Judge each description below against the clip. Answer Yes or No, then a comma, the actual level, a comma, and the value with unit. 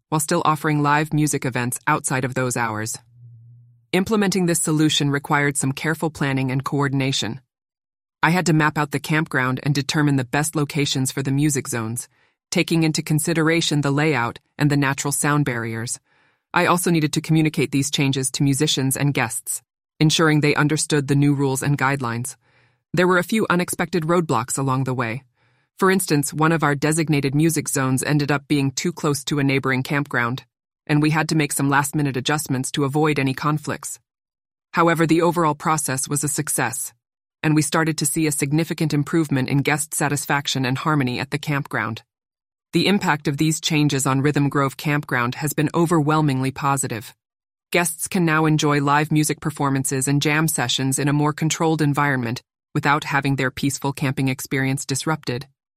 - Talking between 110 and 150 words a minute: No, average, 175 wpm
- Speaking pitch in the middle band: Yes, medium, 145 Hz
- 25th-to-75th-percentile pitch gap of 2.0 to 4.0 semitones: Yes, narrow, 2.6 semitones